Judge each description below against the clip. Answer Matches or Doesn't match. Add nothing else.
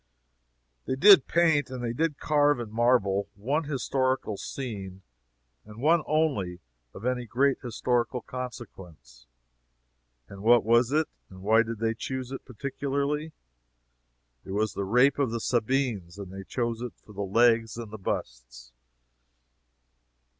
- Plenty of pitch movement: Doesn't match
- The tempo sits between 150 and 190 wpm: Doesn't match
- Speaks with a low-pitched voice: Matches